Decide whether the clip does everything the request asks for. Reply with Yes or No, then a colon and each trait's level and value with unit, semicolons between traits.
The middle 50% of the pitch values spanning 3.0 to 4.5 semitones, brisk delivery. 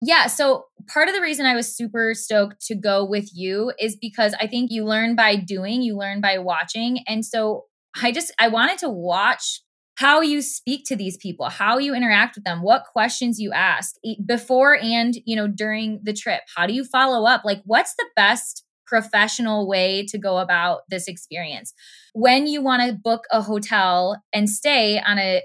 No: average, 3.6 semitones; average, 195 wpm